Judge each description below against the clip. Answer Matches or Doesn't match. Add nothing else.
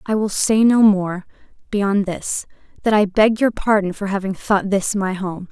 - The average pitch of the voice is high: Matches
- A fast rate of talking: Doesn't match